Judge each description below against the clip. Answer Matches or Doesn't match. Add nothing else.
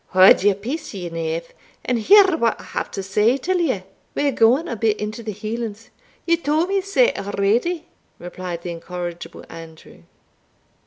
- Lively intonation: Matches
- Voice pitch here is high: Matches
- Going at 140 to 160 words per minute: Doesn't match